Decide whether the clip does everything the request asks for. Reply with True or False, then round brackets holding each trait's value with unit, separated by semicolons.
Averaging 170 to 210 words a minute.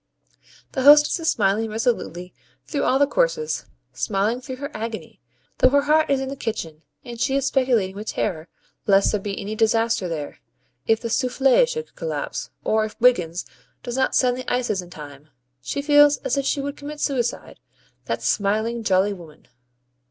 True (175 wpm)